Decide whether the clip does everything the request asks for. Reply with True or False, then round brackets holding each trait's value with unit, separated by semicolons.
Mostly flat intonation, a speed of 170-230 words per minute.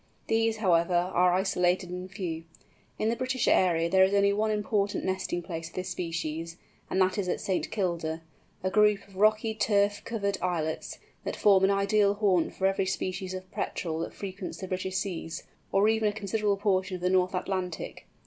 True (2.2 semitones; 185 wpm)